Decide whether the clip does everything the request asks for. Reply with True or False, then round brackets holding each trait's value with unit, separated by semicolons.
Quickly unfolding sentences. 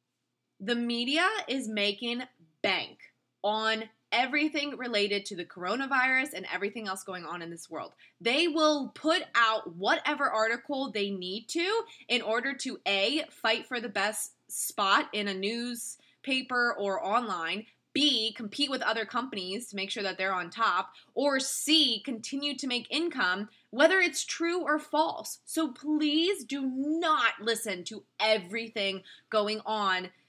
False (145 wpm)